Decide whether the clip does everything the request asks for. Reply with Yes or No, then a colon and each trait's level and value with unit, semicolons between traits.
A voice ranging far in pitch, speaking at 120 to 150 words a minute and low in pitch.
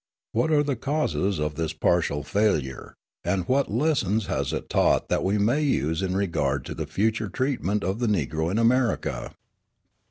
No: wide, 6.9 semitones; average, 170 wpm; low, 100 Hz